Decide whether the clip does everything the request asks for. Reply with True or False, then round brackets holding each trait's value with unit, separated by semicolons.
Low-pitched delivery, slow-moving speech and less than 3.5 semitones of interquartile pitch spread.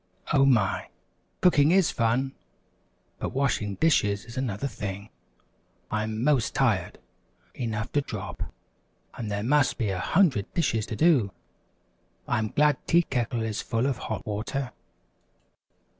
False (120 Hz; 130 wpm; 4.7 semitones)